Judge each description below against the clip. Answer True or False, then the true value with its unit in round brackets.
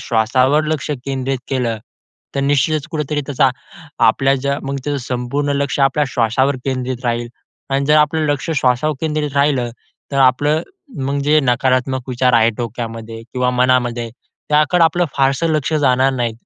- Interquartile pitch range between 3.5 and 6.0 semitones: False (2.7 semitones)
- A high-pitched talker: False (135 Hz)